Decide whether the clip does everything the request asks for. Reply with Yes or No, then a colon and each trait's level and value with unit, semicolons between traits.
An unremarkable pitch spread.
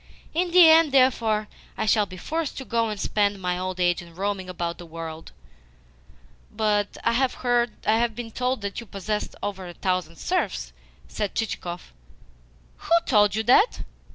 Yes: average, 4.6 semitones